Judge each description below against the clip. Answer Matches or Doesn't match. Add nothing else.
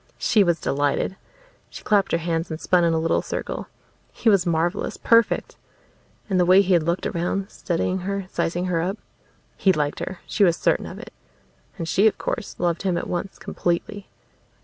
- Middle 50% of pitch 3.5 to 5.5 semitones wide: Doesn't match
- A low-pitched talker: Doesn't match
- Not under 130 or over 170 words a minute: Doesn't match